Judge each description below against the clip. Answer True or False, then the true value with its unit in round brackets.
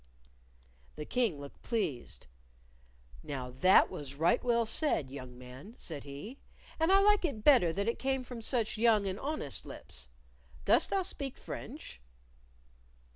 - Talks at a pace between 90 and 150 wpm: True (145 wpm)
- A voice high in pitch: True (210 Hz)